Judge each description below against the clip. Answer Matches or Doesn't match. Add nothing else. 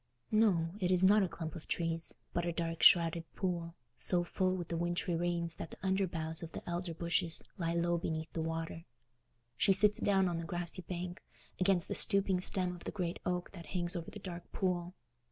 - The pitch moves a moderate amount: Doesn't match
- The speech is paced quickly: Matches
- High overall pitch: Doesn't match